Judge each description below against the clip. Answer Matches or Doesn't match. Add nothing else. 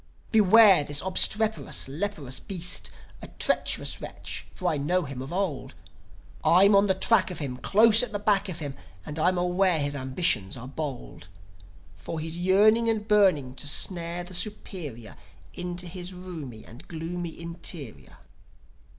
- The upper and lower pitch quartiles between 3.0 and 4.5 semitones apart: Doesn't match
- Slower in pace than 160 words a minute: Matches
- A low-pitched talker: Doesn't match